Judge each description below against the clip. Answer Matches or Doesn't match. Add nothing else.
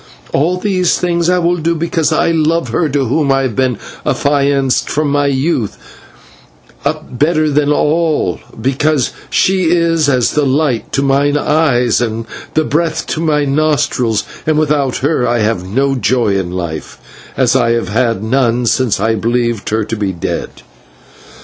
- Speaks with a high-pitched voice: Doesn't match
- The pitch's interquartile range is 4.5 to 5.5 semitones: Matches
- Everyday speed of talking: Matches